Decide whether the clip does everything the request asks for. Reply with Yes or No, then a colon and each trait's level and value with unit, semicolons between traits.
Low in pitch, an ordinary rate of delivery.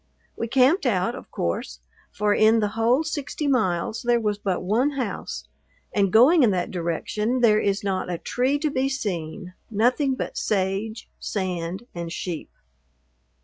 No: high, 215 Hz; average, 155 wpm